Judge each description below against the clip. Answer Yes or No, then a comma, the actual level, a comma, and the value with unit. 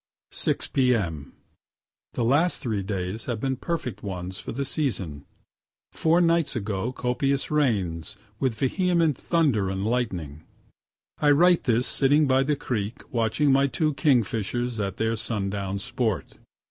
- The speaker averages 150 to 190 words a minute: No, slow, 135 wpm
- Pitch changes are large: Yes, wide, 5.8 semitones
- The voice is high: No, low, 120 Hz